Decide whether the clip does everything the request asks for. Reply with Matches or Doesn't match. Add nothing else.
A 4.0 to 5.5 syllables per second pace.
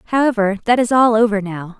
Doesn't match